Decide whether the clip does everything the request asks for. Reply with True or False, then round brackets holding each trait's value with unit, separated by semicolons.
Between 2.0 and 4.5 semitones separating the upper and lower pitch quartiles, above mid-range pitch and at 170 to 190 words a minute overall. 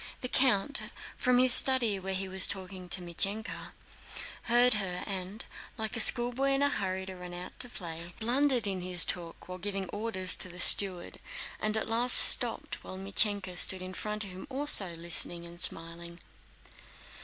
True (4.1 semitones; 195 Hz; 175 wpm)